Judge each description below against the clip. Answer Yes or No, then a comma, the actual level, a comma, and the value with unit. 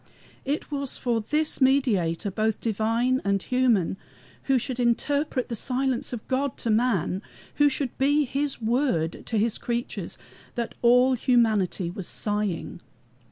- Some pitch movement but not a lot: Yes, average, 3.8 semitones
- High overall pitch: Yes, high, 240 Hz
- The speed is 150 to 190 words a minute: No, average, 140 wpm